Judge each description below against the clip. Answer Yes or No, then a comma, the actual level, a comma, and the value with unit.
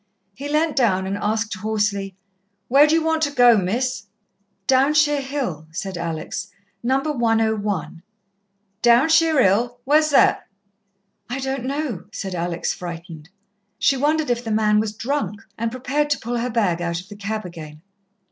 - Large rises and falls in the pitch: Yes, wide, 6.1 semitones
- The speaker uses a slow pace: No, average, 150 wpm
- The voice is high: Yes, high, 225 Hz